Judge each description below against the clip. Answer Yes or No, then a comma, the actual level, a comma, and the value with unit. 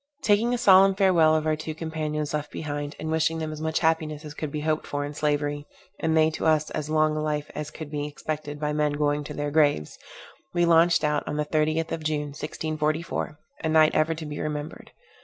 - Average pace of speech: No, fast, 215 wpm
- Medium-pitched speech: Yes, medium, 155 Hz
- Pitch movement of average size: No, narrow, 1.2 semitones